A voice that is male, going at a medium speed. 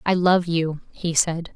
No: female; average, 195 wpm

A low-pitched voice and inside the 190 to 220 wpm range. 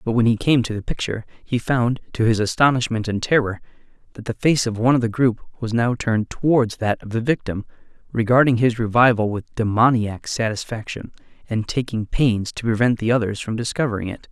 Yes: low, 115 Hz; average, 195 wpm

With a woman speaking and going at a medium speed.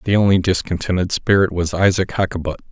No: male; average, 155 wpm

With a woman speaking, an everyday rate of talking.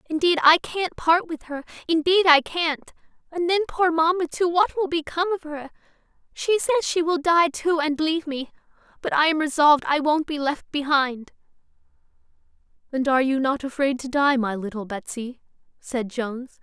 Yes: female; average, 170 wpm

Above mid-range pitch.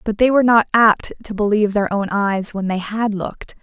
Yes: high, 210 Hz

